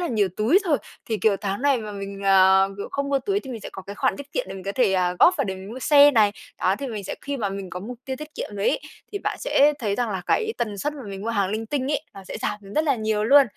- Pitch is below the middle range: No, high, 220 Hz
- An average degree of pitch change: No, wide, 6.1 semitones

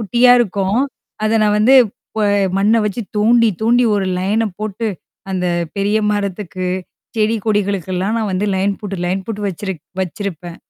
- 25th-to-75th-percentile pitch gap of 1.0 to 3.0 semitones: Yes, narrow, 2.6 semitones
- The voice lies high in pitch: Yes, high, 205 Hz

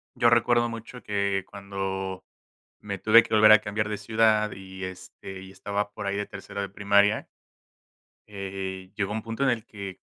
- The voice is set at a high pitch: No, low, 100 Hz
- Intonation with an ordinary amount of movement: No, narrow, 2.0 semitones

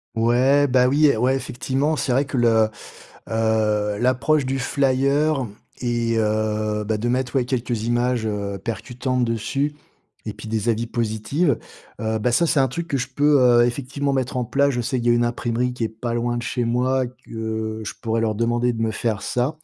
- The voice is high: No, low, 120 Hz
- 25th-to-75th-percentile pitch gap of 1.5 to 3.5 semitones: Yes, average, 2.9 semitones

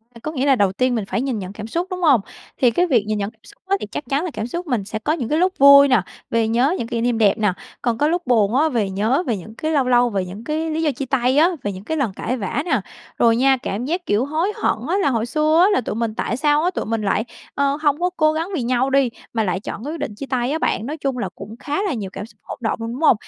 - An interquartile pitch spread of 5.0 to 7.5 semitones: Yes, wide, 5.5 semitones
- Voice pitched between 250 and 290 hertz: Yes, very high, 255 Hz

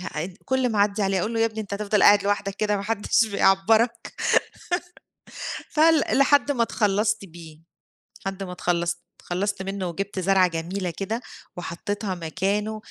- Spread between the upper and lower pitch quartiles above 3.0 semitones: No, average, 2.7 semitones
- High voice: Yes, high, 200 Hz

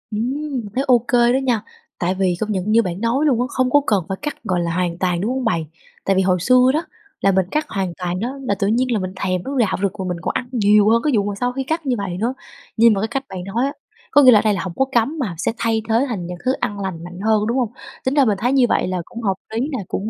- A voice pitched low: No, high, 220 Hz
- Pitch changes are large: No, average, 5.0 semitones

